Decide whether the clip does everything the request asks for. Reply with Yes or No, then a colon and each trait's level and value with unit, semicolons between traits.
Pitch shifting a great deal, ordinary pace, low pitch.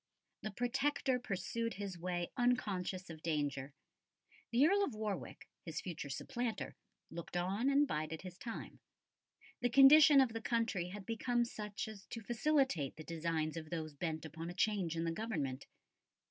No: wide, 6.4 semitones; average, 160 wpm; high, 195 Hz